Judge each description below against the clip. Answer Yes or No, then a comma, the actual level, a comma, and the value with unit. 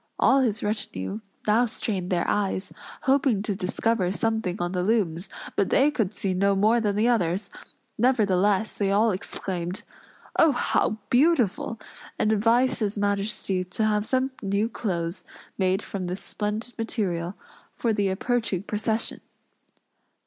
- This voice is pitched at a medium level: No, high, 210 Hz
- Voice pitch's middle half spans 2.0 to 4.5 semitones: Yes, average, 3.2 semitones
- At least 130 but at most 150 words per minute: Yes, average, 140 wpm